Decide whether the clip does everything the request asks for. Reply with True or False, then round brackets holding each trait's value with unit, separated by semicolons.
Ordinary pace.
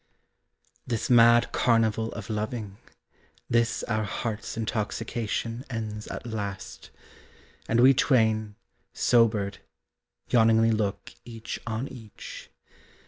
False (95 wpm)